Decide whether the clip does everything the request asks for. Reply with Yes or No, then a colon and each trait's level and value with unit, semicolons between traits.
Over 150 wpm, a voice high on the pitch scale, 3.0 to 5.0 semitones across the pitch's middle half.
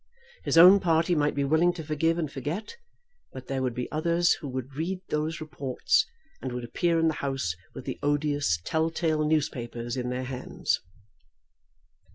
No: average, 175 wpm; medium, 150 Hz; average, 3.8 semitones